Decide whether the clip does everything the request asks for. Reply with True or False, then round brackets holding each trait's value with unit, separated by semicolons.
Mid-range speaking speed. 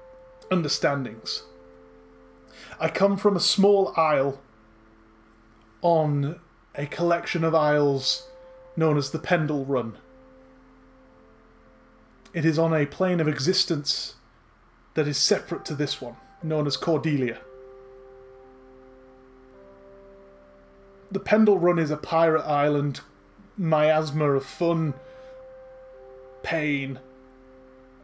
False (95 wpm)